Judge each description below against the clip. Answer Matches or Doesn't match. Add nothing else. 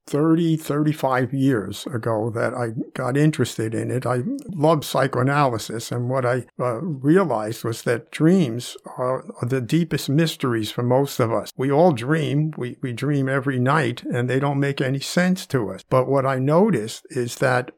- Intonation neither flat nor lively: Matches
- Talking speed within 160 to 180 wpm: Matches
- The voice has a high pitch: Doesn't match